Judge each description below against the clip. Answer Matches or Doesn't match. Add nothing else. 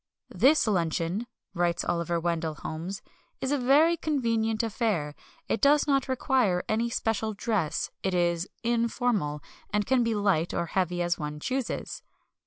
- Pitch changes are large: Matches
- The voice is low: Doesn't match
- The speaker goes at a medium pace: Matches